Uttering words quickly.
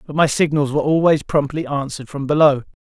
No: average, 190 wpm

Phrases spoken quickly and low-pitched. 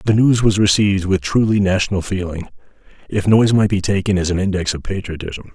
No: average, 195 wpm; low, 100 Hz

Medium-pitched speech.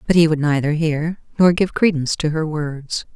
Yes: medium, 155 Hz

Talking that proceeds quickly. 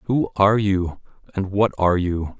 No: average, 175 wpm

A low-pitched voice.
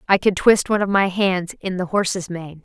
No: high, 190 Hz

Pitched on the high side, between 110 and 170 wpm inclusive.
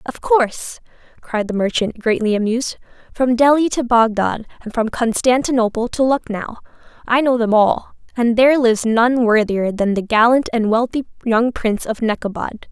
Yes: high, 230 Hz; average, 160 wpm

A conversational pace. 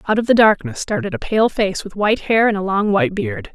No: fast, 255 wpm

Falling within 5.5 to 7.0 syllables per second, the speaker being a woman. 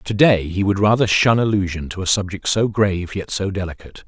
No: 5.7 syllables/s; male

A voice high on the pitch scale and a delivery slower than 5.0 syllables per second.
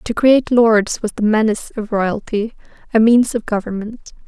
Yes: high, 220 Hz; 4.8 syllables/s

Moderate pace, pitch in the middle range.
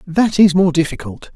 Yes: average, 175 wpm; medium, 175 Hz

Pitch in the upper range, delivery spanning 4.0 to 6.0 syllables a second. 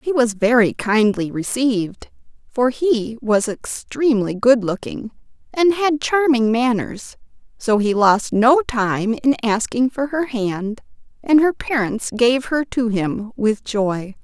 No: high, 235 Hz; 3.7 syllables/s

